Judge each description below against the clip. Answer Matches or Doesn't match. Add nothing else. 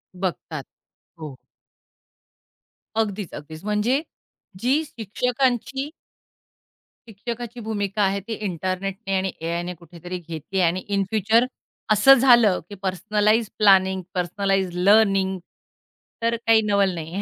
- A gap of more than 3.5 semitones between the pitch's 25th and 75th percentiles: Doesn't match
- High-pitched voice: Matches